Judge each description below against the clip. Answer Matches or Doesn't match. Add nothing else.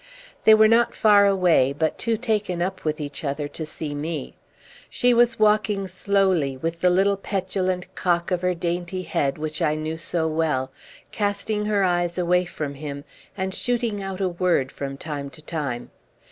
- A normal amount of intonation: Matches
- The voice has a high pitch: Doesn't match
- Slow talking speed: Doesn't match